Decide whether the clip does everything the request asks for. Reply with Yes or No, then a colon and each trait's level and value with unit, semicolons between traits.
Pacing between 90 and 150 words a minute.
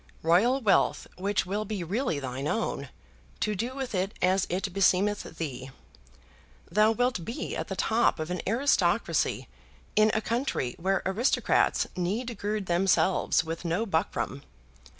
Yes: average, 145 wpm